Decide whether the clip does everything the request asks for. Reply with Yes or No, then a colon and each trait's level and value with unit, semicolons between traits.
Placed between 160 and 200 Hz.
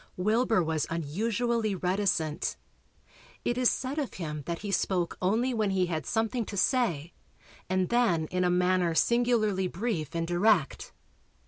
Yes: high, 190 Hz